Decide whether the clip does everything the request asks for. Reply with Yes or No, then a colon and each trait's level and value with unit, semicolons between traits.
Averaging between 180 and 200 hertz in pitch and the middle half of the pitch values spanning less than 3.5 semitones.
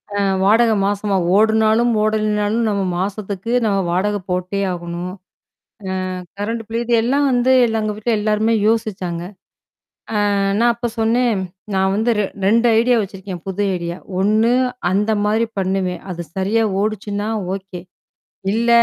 No: high, 210 Hz; average, 2.8 semitones